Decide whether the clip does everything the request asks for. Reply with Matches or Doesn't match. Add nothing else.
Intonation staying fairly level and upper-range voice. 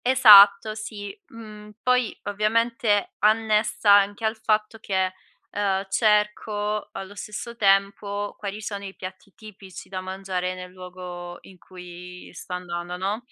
Matches